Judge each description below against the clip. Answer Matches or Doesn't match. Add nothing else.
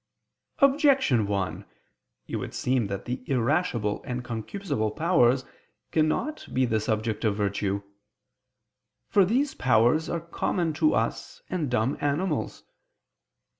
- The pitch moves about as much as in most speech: Doesn't match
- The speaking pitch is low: Matches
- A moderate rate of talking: Doesn't match